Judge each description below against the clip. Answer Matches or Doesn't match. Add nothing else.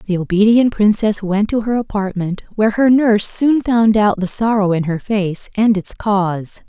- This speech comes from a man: Doesn't match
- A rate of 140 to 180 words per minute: Doesn't match